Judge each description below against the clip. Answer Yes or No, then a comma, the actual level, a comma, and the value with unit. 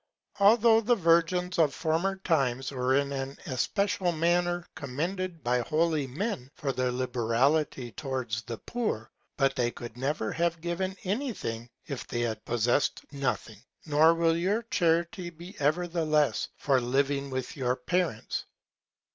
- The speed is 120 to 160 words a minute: Yes, average, 145 wpm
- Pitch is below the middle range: No, medium, 150 Hz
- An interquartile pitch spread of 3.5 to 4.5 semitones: No, wide, 5.4 semitones